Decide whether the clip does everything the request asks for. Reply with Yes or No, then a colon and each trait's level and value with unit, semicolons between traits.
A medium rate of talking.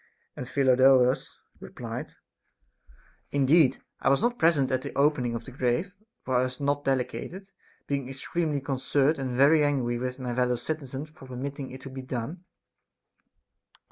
Yes: average, 150 wpm